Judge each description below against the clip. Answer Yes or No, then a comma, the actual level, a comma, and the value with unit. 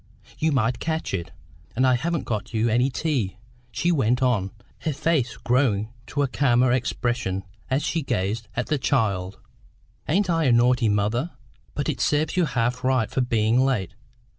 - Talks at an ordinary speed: Yes, average, 170 wpm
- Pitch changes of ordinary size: Yes, average, 4.4 semitones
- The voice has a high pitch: No, low, 125 Hz